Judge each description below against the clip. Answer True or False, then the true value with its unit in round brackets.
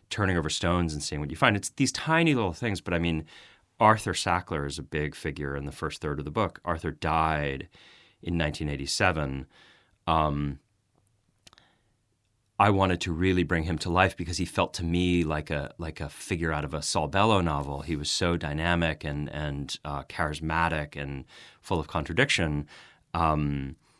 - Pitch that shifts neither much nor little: True (3.2 semitones)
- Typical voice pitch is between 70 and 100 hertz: True (80 Hz)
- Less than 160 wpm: False (180 wpm)